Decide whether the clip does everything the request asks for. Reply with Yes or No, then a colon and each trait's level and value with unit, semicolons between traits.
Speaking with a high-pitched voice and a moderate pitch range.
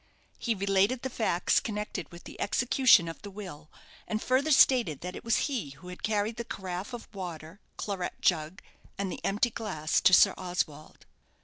Yes: high, 195 Hz; average, 4.2 semitones